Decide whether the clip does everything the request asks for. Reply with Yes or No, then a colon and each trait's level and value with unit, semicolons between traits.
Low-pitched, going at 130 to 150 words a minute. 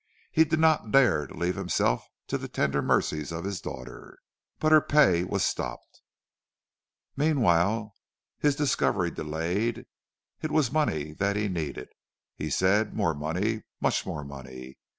Yes: very low, 95 Hz; average, 145 wpm